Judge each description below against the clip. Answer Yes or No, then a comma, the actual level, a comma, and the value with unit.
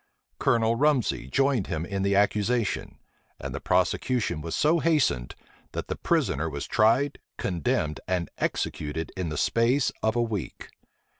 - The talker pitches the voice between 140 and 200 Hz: No, low, 105 Hz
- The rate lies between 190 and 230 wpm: No, average, 145 wpm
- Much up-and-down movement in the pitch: Yes, wide, 7.1 semitones